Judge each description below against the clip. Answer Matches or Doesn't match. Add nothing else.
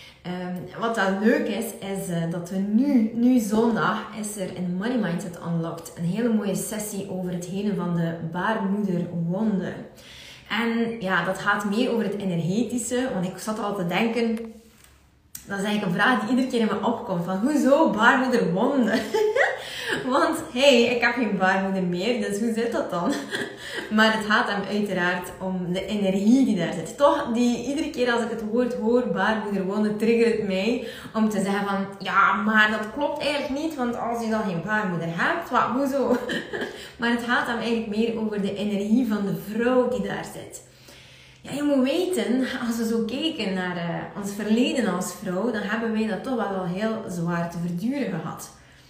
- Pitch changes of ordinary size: Matches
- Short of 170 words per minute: Doesn't match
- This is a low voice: Doesn't match